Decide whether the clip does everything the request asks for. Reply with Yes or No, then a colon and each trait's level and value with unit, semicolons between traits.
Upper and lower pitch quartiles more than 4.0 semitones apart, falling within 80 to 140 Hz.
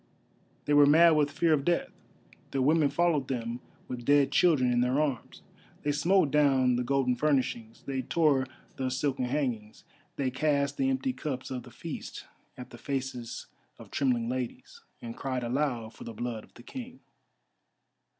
No: average, 3.1 semitones; low, 135 Hz